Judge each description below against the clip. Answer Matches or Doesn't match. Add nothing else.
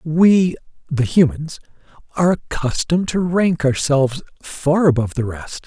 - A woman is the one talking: Doesn't match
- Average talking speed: Doesn't match